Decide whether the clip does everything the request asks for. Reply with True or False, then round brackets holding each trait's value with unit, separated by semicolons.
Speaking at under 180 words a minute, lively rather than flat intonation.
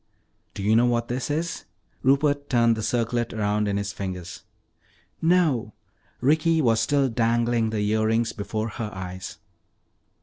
False (140 wpm; 3.5 semitones)